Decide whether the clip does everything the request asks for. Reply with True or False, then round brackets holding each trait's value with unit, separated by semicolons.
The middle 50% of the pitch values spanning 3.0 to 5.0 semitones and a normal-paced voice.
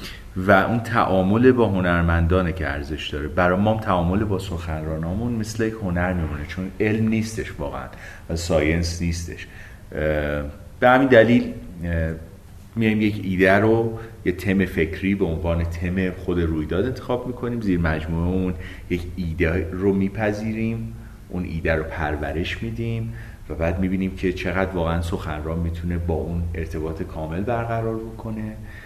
True (4.3 semitones; 140 wpm)